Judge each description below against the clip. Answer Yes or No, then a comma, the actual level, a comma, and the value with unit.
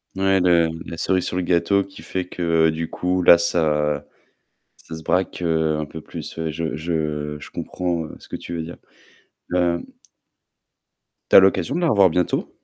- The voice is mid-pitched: No, very low, 85 Hz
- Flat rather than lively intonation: Yes, narrow, 2.2 semitones